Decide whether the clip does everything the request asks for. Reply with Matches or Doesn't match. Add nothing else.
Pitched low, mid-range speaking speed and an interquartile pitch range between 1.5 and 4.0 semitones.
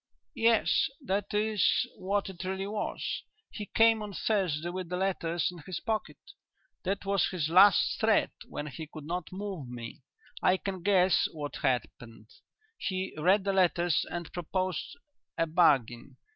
Doesn't match